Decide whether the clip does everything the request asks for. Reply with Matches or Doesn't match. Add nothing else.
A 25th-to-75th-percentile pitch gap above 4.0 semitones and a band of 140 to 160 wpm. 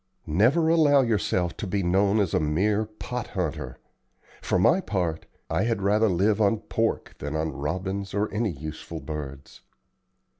Matches